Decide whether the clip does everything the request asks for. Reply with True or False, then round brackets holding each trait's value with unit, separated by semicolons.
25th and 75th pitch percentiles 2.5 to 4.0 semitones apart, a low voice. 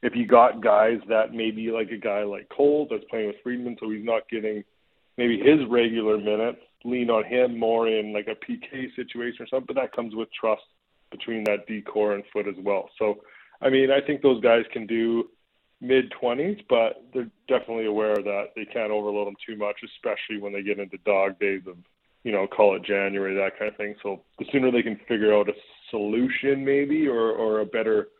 True (3.0 semitones; 115 Hz)